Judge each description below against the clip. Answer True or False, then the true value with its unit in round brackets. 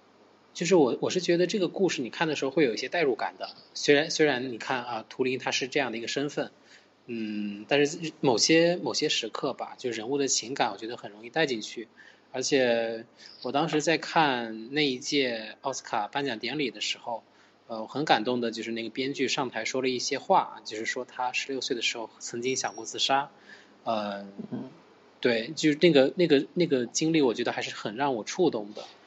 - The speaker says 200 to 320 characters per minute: True (300 characters per minute)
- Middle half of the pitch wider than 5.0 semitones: False (4.5 semitones)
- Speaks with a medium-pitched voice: False (130 Hz)